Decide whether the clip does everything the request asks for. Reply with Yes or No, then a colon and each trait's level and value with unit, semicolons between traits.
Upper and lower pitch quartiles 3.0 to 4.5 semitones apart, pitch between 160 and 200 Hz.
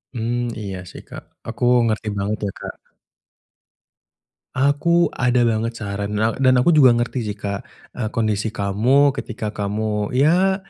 No: average, 3.5 semitones; low, 115 Hz